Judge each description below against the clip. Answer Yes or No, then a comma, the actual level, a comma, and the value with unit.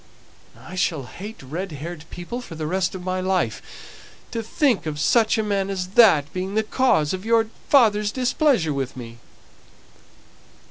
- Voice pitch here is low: No, medium, 185 Hz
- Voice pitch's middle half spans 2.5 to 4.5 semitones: No, wide, 5.6 semitones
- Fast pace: No, average, 165 wpm